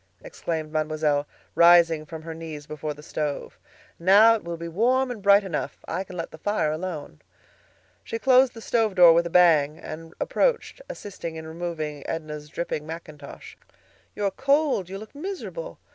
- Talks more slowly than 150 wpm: No, average, 170 wpm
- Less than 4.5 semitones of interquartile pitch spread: No, average, 4.9 semitones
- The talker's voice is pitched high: No, medium, 170 Hz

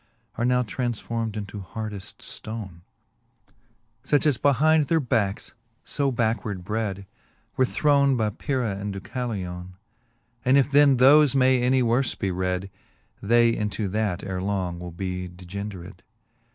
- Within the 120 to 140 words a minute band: Yes, slow, 135 wpm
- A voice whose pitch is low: Yes, low, 110 Hz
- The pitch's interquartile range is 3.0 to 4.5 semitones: No, average, 4.9 semitones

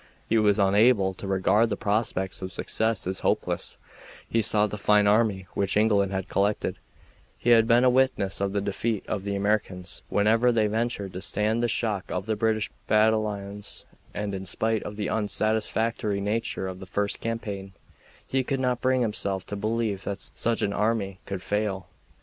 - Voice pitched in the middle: No, low, 105 Hz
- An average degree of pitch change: No, narrow, 2.2 semitones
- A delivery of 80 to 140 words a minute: No, average, 180 wpm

